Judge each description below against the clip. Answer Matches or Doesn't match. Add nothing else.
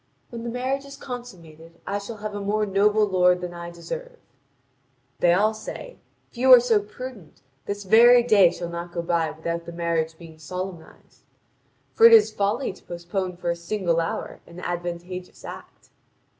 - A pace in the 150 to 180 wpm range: Matches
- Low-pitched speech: Doesn't match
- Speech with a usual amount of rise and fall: Matches